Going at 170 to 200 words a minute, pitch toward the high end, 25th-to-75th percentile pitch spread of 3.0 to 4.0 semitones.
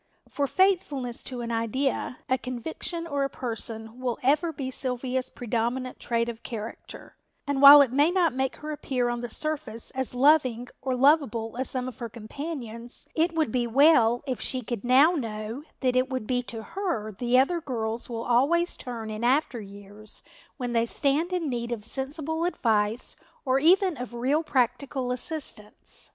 Yes: average, 175 wpm; very high, 255 Hz; average, 3.5 semitones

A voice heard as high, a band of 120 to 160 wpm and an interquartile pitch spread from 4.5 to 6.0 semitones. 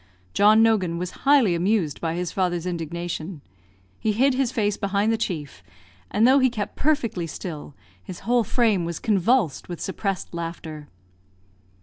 Yes: high, 195 Hz; average, 150 wpm; average, 4.8 semitones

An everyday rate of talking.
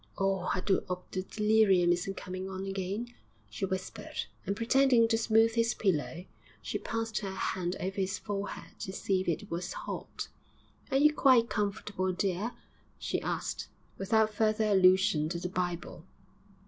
Yes: average, 160 wpm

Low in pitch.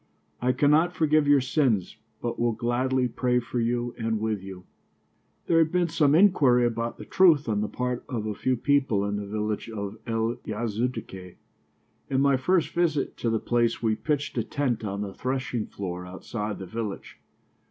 Yes: low, 120 Hz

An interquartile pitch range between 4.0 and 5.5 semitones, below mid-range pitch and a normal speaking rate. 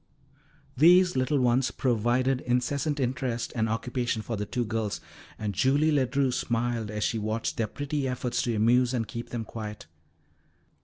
No: average, 2.7 semitones; low, 120 Hz; average, 155 wpm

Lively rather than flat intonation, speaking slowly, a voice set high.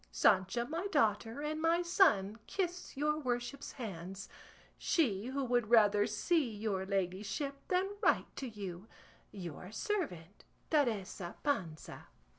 Yes: wide, 7.4 semitones; slow, 120 wpm; high, 230 Hz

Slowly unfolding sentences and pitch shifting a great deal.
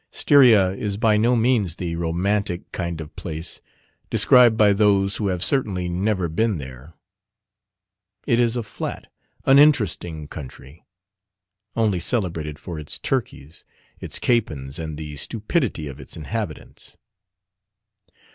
Yes: slow, 125 wpm; wide, 5.7 semitones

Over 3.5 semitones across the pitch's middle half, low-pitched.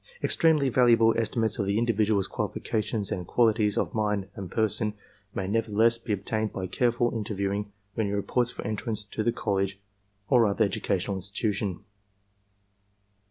No: narrow, 2.5 semitones; low, 105 Hz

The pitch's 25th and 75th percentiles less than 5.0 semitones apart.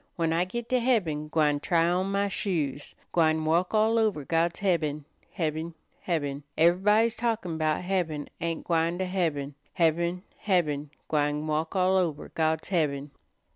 Yes: average, 3.4 semitones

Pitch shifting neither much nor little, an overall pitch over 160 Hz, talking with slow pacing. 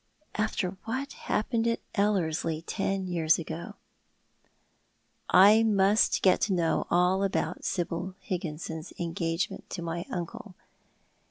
Yes: average, 3.6 semitones; medium, 185 Hz; slow, 110 wpm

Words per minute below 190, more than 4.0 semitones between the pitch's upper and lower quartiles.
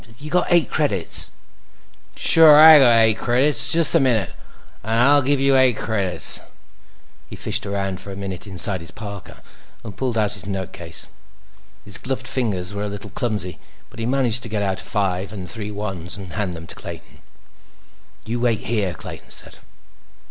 Yes: average, 180 wpm; average, 4.4 semitones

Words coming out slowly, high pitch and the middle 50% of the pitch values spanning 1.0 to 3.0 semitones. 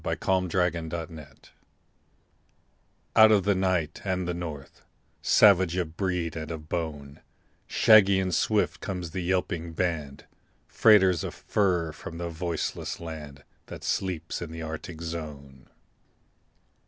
No: slow, 130 wpm; very low, 85 Hz; average, 2.7 semitones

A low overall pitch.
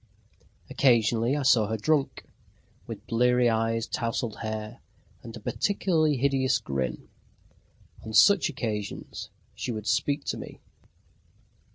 Yes: low, 115 Hz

